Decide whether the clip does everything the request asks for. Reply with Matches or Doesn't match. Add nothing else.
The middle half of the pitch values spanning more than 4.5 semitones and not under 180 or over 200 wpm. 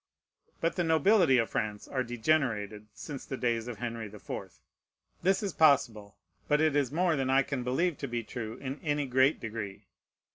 Matches